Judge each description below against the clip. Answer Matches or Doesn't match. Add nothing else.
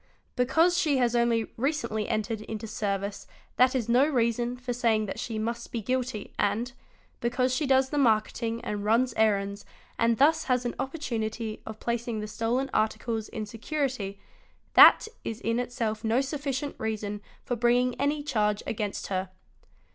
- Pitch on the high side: Matches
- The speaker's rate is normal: Matches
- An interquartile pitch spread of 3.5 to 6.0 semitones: Doesn't match